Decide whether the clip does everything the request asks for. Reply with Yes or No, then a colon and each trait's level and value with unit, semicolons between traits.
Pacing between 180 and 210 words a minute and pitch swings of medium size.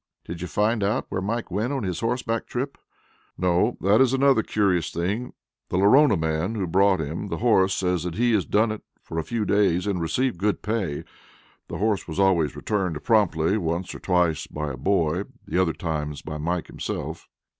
Yes: average, 190 wpm; average, 4.5 semitones